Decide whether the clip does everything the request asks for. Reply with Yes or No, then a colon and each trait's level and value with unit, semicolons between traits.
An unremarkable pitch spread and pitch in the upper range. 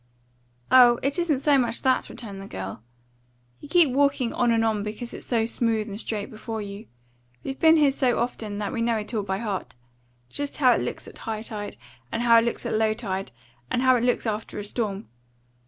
Yes: average, 3.2 semitones; high, 230 Hz